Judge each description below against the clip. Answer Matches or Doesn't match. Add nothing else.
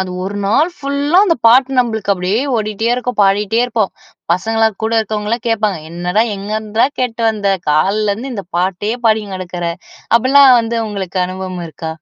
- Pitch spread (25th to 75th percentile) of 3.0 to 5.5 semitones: Matches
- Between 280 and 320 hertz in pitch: Doesn't match